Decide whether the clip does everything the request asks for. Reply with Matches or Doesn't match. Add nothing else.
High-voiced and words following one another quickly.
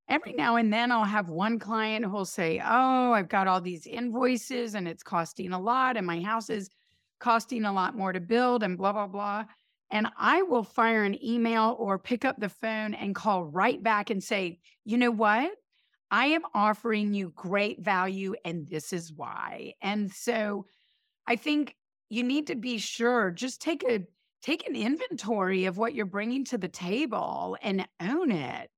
Doesn't match